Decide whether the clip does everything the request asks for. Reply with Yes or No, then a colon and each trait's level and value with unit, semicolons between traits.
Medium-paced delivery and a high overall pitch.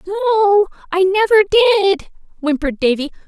No: slow, 110 wpm; very high, 380 Hz